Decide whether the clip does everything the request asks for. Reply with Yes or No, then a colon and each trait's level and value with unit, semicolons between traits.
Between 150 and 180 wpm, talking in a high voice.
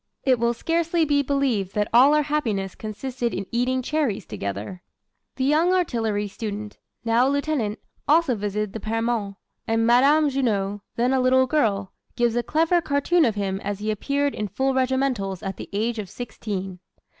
Yes: average, 170 wpm; high, 235 Hz